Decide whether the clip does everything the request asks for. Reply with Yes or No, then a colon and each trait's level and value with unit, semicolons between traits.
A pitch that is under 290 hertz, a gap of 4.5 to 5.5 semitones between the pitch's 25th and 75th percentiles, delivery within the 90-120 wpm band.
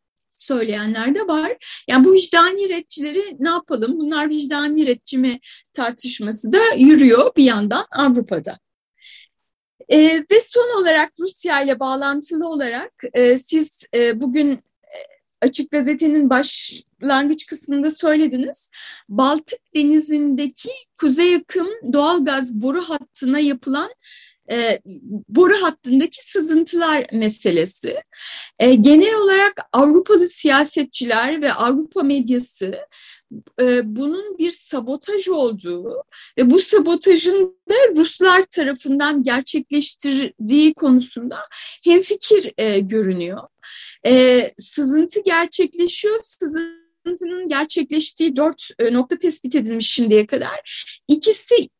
No: very high, 295 Hz; average, 5.0 semitones; average, 100 wpm